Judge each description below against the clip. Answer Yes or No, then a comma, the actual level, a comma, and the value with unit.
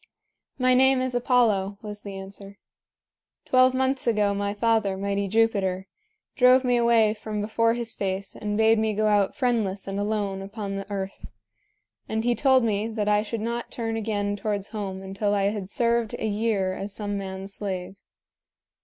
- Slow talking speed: No, average, 170 wpm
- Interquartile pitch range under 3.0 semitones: Yes, narrow, 2.5 semitones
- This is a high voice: Yes, high, 210 Hz